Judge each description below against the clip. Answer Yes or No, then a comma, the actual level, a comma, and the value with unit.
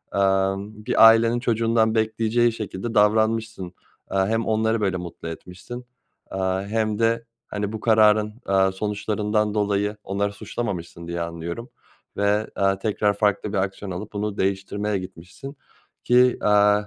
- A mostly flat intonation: Yes, narrow, 2.3 semitones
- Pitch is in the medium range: No, low, 105 Hz